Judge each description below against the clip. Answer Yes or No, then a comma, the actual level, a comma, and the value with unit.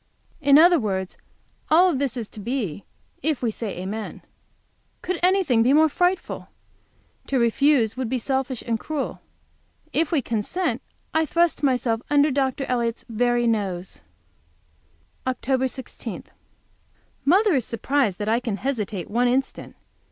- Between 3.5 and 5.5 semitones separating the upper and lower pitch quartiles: Yes, average, 4.4 semitones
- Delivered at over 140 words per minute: No, slow, 135 wpm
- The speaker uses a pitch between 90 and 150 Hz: No, very high, 255 Hz